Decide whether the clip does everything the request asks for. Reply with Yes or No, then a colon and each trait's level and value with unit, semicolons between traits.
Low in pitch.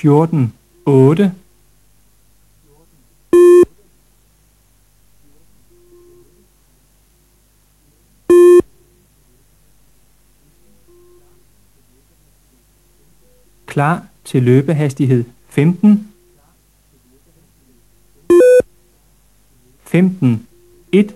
No: medium, 165 Hz